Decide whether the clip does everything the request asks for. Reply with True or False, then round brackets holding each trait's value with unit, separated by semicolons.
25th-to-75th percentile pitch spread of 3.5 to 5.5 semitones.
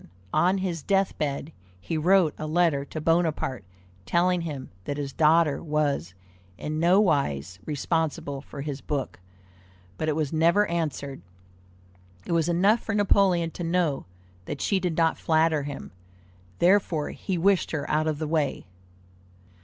False (3.1 semitones)